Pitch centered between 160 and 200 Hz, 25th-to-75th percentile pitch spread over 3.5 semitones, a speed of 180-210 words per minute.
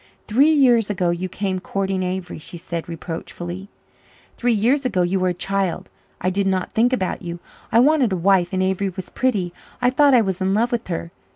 Yes: high, 190 Hz; average, 4.3 semitones; fast, 205 wpm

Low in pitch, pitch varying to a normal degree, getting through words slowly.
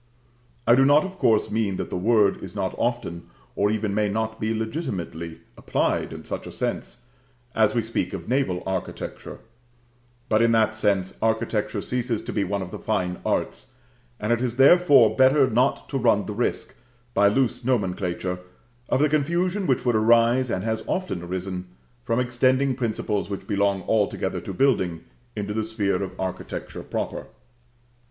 No: low, 110 Hz; average, 4.2 semitones; average, 170 wpm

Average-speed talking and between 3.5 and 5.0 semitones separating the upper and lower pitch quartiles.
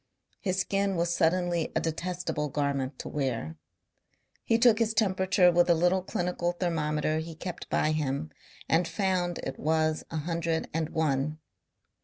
No: average, 150 wpm; average, 2.9 semitones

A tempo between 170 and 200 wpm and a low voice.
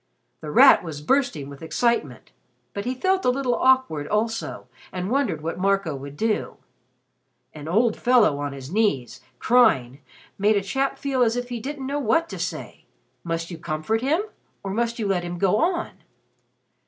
No: average, 175 wpm; high, 210 Hz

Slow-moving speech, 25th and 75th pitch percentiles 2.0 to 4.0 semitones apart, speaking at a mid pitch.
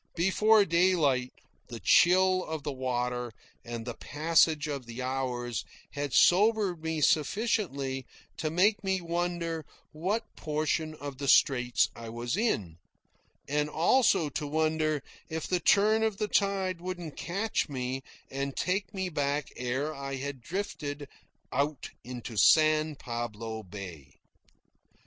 No: slow, 130 wpm; wide, 5.6 semitones; medium, 150 Hz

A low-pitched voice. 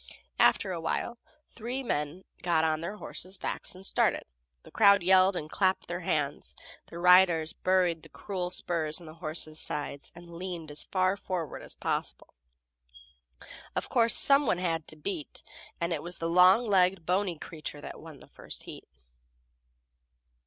No: medium, 175 Hz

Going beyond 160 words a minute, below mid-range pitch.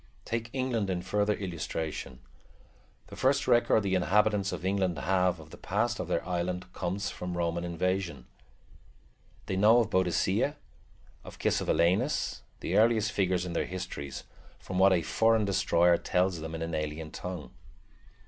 No: average, 150 wpm; very low, 95 Hz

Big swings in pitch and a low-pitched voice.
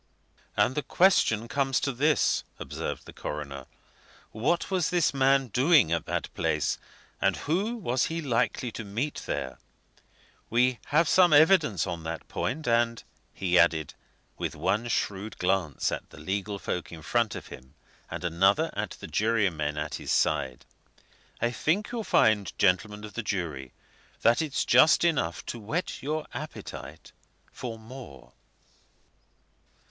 Yes: wide, 8.1 semitones; low, 115 Hz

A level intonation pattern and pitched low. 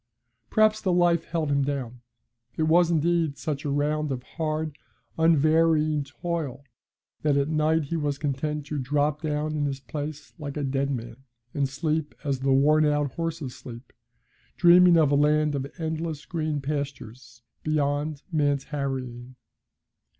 No: narrow, 2.1 semitones; medium, 150 Hz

